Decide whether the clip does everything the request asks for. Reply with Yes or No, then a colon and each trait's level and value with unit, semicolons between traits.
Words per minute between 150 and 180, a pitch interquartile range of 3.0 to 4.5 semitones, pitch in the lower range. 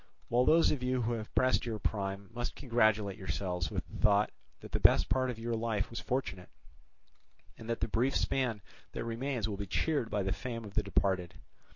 No: fast, 205 wpm; average, 3.4 semitones; low, 115 Hz